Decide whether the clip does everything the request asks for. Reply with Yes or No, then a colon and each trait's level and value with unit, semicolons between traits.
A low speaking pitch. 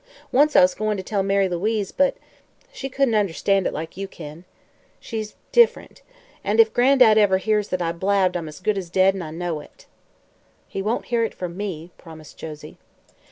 No: high, 195 Hz